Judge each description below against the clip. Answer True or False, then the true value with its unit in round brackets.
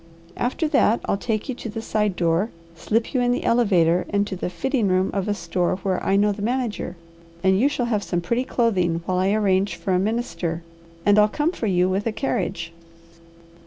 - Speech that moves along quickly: True (210 wpm)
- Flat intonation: False (4.0 semitones)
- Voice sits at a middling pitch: False (205 Hz)